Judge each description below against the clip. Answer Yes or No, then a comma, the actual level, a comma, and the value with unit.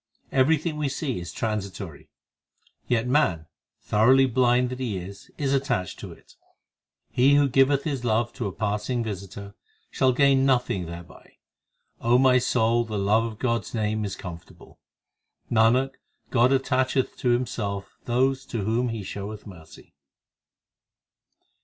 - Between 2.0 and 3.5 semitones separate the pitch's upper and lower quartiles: No, average, 4.3 semitones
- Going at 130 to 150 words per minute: Yes, average, 140 wpm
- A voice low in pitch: Yes, low, 120 Hz